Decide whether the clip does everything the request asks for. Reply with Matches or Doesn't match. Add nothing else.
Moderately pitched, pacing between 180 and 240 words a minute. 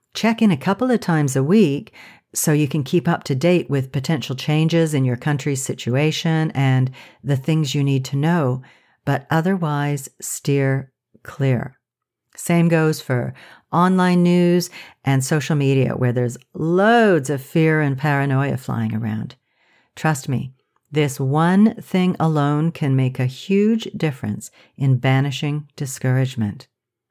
Doesn't match